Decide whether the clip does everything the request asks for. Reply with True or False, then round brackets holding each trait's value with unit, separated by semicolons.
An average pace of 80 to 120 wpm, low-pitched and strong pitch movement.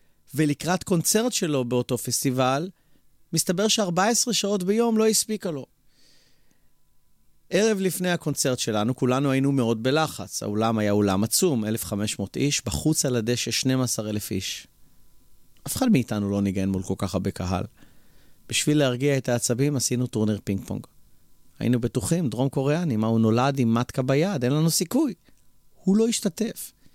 False (145 wpm; 130 Hz; 7.2 semitones)